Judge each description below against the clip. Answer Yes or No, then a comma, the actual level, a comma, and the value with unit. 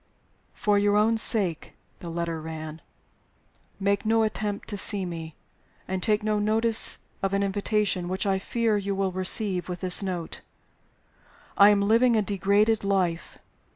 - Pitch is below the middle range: No, high, 200 Hz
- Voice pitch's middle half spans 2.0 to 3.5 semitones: Yes, narrow, 2.5 semitones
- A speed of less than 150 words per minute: No, average, 155 wpm